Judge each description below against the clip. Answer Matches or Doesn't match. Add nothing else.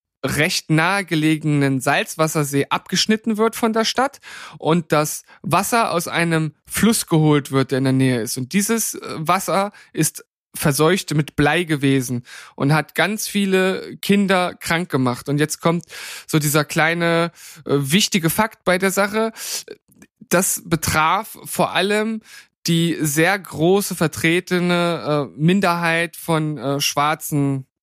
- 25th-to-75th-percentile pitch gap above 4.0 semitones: Matches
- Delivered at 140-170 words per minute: Doesn't match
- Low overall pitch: Doesn't match